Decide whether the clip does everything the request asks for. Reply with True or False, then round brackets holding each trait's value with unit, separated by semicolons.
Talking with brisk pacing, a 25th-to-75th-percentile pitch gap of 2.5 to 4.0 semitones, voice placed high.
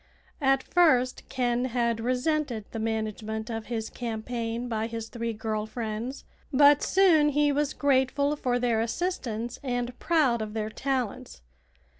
False (140 wpm; 3.4 semitones; 245 Hz)